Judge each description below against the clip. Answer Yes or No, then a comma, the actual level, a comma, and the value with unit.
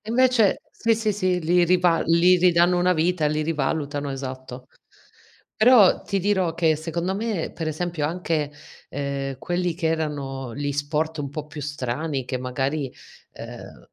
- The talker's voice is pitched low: No, medium, 160 Hz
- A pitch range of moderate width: Yes, average, 3.8 semitones